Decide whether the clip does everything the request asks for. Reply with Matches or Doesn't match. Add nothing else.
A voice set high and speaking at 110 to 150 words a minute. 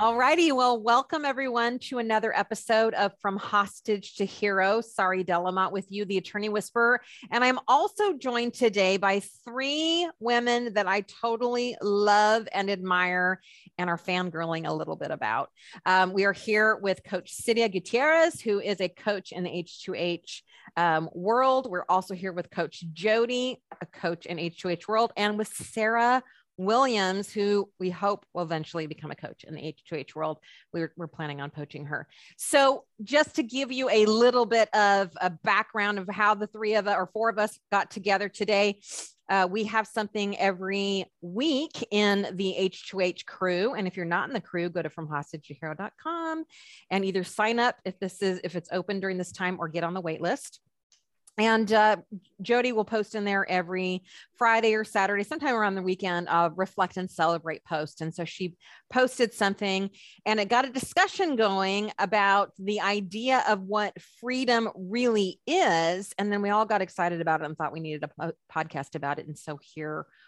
Doesn't match